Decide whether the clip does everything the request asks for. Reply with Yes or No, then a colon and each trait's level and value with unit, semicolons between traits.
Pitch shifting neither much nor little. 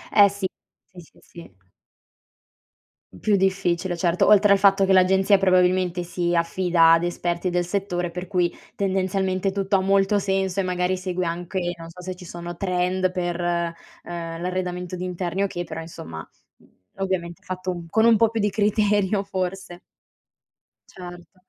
No: narrow, 1.8 semitones